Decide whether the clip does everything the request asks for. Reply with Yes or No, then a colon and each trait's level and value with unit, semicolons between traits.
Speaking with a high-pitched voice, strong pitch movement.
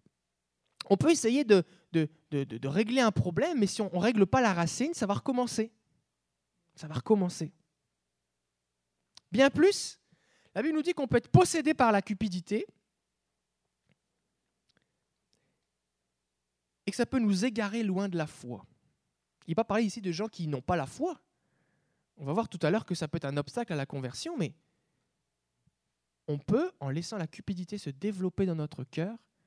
No: medium, 180 Hz; wide, 7.7 semitones